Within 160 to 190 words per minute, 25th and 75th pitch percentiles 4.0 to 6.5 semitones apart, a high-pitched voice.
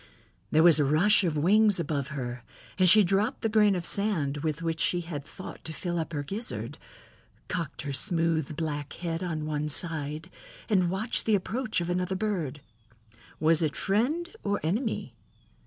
No: average, 170 wpm; average, 4.7 semitones; medium, 170 Hz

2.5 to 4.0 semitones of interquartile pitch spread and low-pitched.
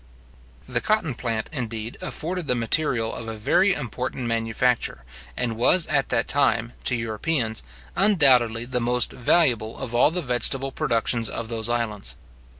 Yes: average, 3.1 semitones; low, 120 Hz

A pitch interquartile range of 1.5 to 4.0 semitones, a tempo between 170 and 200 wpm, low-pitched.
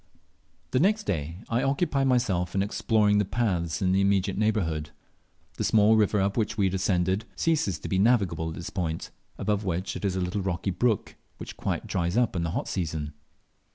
Yes: average, 3.7 semitones; average, 195 wpm; very low, 95 Hz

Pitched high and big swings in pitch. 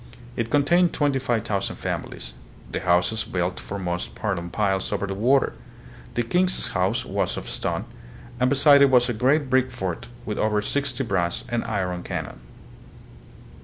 No: low, 115 Hz; wide, 5.8 semitones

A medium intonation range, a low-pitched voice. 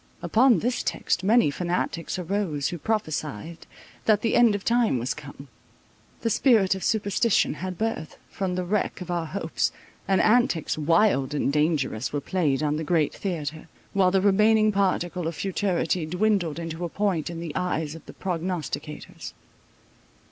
No: average, 4.3 semitones; medium, 180 Hz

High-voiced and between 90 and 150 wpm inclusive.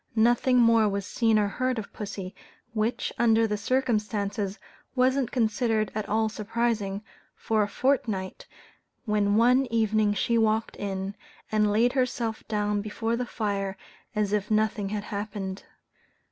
Yes: high, 215 Hz; average, 140 wpm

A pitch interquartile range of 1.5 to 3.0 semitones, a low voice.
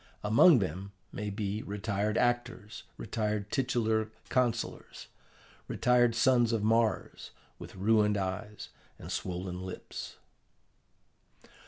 Yes: average, 2.7 semitones; low, 110 Hz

